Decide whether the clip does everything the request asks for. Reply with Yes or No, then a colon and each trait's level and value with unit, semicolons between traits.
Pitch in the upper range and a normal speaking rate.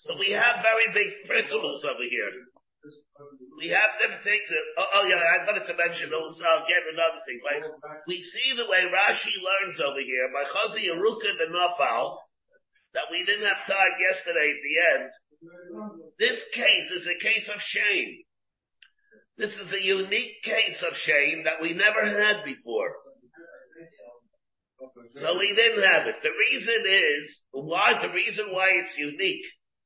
Yes: high, 195 Hz; average, 165 wpm